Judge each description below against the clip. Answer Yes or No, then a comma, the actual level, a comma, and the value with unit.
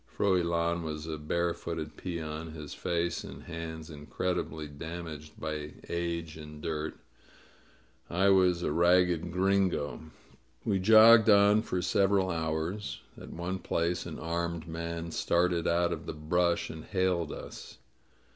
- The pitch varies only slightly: Yes, narrow, 2.3 semitones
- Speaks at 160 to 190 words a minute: No, average, 140 wpm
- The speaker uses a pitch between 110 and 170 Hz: No, very low, 85 Hz